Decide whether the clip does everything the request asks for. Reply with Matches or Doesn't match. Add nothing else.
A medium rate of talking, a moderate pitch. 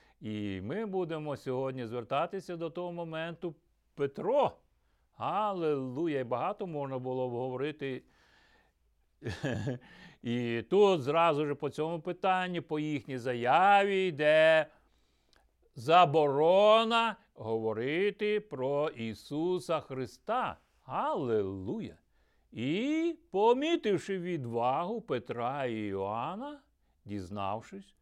Doesn't match